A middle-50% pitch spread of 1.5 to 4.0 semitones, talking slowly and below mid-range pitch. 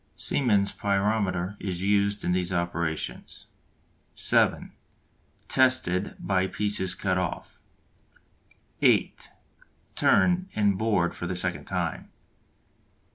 Yes: narrow, 2.5 semitones; slow, 95 wpm; very low, 95 Hz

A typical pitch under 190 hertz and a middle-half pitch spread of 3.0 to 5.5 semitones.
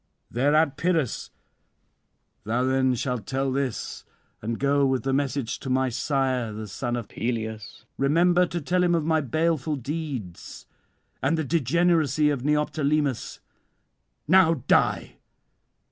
Yes: medium, 140 Hz; average, 3.9 semitones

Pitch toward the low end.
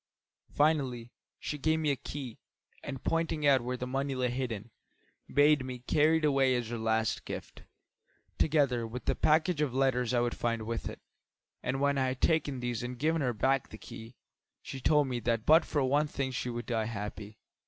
Yes: low, 130 Hz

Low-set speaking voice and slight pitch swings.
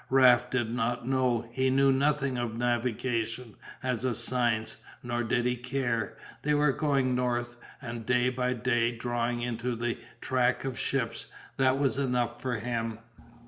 Yes: low, 125 Hz; narrow, 1.5 semitones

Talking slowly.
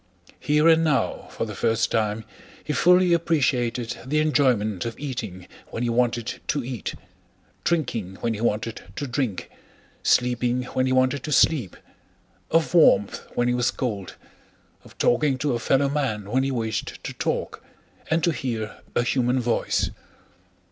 No: average, 155 wpm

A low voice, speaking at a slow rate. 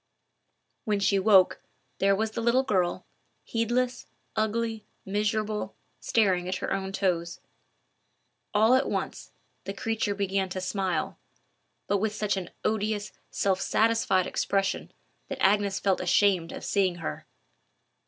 No: high, 200 Hz; slow, 130 wpm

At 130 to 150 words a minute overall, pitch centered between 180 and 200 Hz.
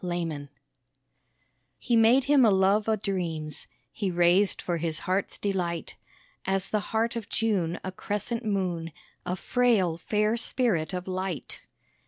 Yes: average, 145 wpm; high, 190 Hz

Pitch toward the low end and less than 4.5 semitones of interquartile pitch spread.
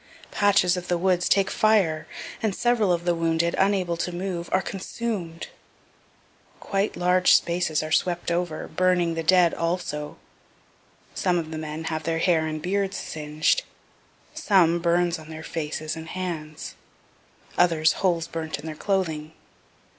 No: medium, 170 Hz; narrow, 2.5 semitones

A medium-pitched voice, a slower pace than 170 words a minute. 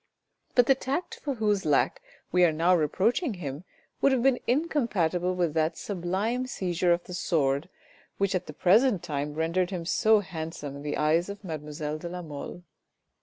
No: medium, 180 Hz; average, 175 wpm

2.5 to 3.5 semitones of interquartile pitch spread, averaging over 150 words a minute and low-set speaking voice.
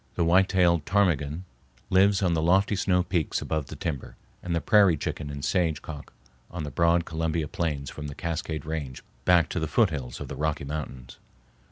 Yes: average, 3.1 semitones; average, 190 wpm; very low, 80 Hz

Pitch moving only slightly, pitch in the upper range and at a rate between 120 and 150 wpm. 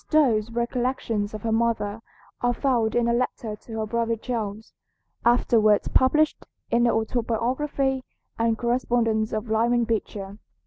Yes: narrow, 1.8 semitones; high, 230 Hz; slow, 135 wpm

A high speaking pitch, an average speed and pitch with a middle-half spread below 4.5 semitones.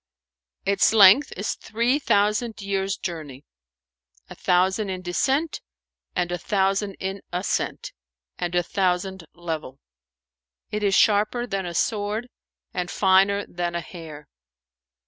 No: high, 195 Hz; slow, 125 wpm; average, 2.8 semitones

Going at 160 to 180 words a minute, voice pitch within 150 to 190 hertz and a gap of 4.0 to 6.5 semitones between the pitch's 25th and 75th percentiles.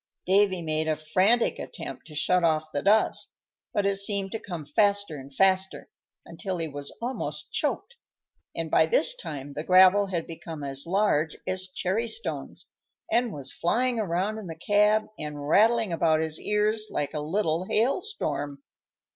Yes: average, 165 wpm; medium, 185 Hz; average, 5.2 semitones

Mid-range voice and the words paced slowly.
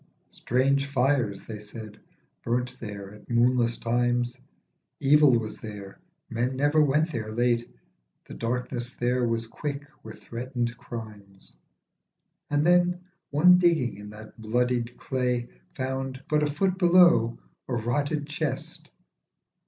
No: low, 125 Hz; slow, 125 wpm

